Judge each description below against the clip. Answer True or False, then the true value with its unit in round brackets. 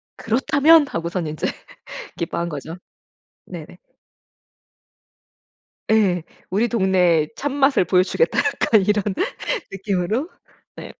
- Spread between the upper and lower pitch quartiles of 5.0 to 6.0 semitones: True (5.6 semitones)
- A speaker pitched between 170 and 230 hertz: True (190 Hz)